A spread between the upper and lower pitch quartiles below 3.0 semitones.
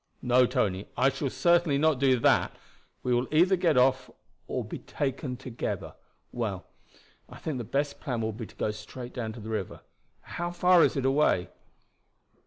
No: average, 4.2 semitones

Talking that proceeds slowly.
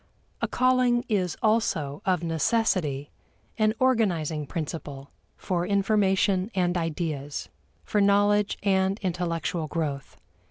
Yes: slow, 105 wpm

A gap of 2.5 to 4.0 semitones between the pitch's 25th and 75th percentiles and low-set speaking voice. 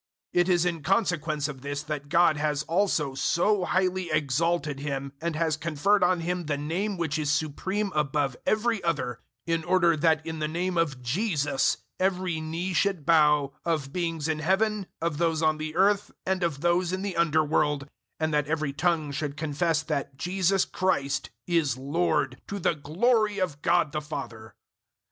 No: average, 3.3 semitones; medium, 160 Hz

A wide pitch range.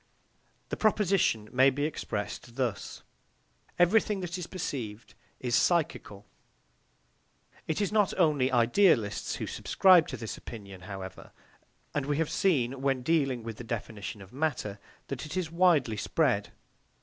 Yes: wide, 7.0 semitones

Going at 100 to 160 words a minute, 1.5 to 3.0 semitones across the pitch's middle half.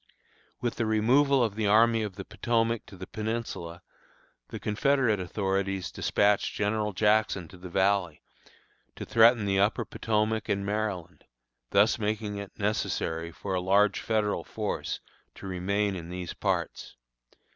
Yes: average, 145 wpm; narrow, 2.4 semitones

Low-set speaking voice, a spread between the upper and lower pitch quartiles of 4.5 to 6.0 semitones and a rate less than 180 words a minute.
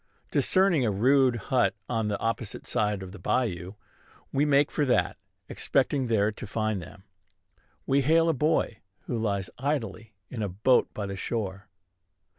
Yes: low, 115 Hz; average, 4.8 semitones; average, 160 wpm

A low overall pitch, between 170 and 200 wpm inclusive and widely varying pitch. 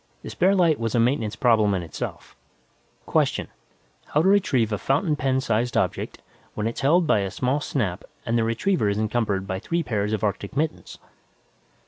Yes: low, 115 Hz; average, 180 wpm; wide, 5.8 semitones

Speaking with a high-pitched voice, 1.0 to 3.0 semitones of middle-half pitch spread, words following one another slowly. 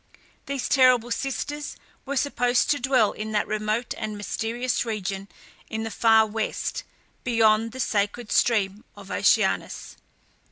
Yes: high, 225 Hz; average, 2.7 semitones; slow, 130 wpm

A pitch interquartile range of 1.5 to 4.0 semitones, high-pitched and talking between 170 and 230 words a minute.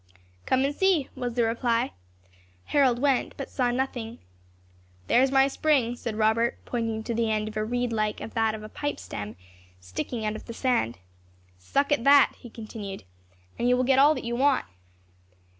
Yes: average, 3.3 semitones; high, 240 Hz; average, 185 wpm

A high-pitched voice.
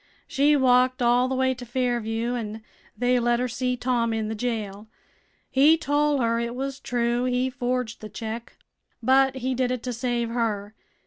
Yes: high, 245 Hz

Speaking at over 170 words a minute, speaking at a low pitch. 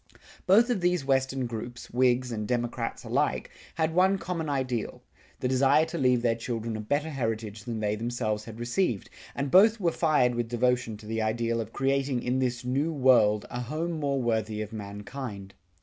Yes: average, 180 wpm; low, 125 Hz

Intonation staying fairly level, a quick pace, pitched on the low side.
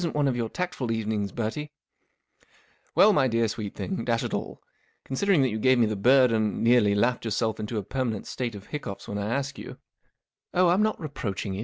No: average, 4.3 semitones; fast, 230 wpm; low, 120 Hz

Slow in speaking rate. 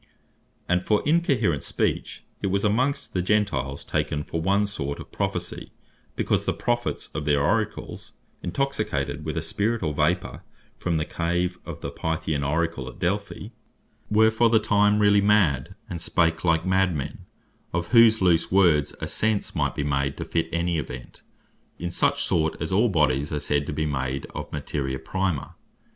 No: average, 170 wpm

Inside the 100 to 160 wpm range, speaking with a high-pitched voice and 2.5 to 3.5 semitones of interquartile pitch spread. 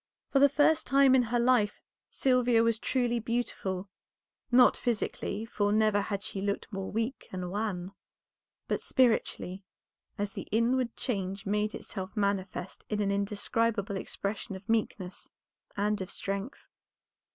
Yes: average, 140 wpm; high, 210 Hz; average, 3.1 semitones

